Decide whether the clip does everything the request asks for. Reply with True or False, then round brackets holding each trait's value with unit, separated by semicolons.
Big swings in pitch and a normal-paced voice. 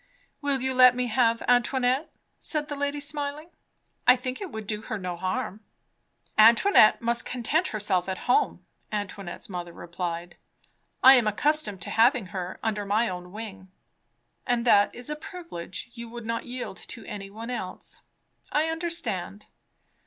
False (4.8 semitones; 155 wpm)